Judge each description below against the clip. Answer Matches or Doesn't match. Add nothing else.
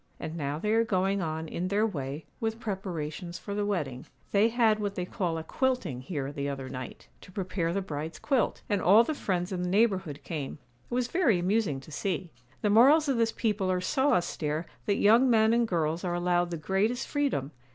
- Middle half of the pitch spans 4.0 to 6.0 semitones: Matches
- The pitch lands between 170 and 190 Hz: Matches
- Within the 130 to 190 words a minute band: Doesn't match